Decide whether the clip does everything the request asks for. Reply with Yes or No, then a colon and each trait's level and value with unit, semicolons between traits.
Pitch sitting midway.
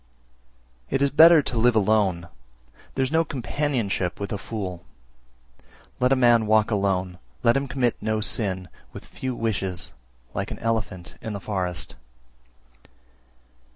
No: low, 110 Hz